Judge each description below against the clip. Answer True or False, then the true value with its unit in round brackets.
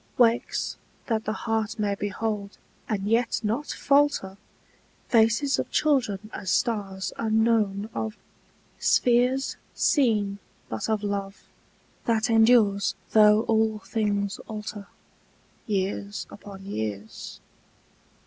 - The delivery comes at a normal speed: False (100 wpm)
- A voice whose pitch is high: True (215 Hz)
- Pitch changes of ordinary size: False (2.2 semitones)